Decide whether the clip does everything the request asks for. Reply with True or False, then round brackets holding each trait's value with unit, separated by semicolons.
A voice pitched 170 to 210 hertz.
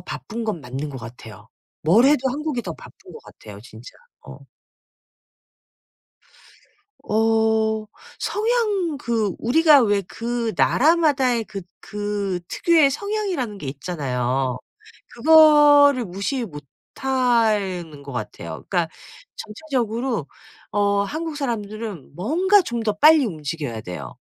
False (220 Hz)